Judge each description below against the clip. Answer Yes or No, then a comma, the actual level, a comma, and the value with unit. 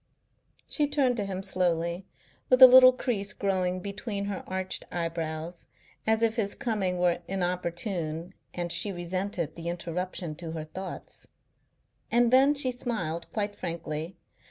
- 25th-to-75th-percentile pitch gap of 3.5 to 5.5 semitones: Yes, average, 4.2 semitones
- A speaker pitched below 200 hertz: Yes, medium, 185 Hz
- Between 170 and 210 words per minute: No, average, 140 wpm